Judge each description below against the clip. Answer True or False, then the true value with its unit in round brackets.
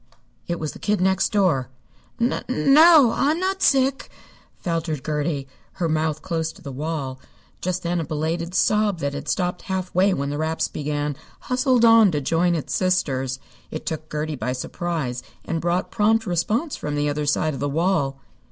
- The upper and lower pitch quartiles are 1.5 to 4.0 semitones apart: False (4.8 semitones)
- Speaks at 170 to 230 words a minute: True (175 wpm)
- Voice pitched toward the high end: False (165 Hz)